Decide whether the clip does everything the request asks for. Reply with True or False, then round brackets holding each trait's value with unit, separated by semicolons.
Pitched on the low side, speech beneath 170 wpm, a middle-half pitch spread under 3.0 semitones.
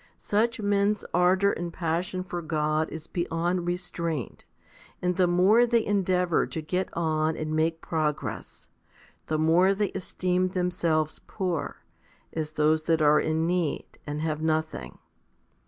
False (170 Hz; 140 wpm; 2.6 semitones)